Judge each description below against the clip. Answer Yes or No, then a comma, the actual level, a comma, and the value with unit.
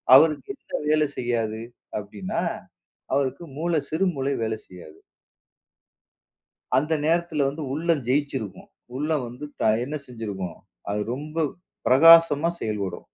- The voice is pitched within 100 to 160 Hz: Yes, medium, 140 Hz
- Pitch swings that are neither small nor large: No, wide, 5.9 semitones